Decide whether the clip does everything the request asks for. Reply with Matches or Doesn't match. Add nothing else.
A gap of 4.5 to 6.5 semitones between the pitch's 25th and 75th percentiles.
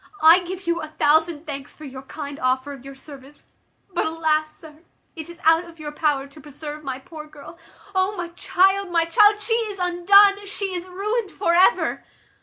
Doesn't match